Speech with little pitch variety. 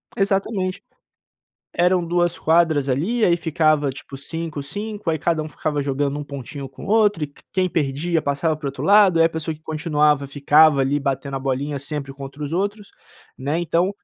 No: average, 3.6 semitones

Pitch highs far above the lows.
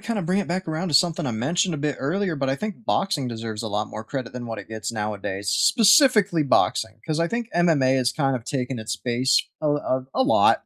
Yes: wide, 7.6 semitones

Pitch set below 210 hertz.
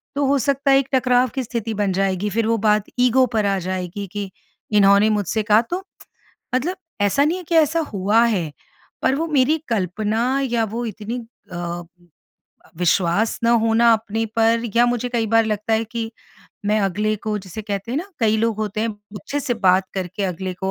No: high, 220 Hz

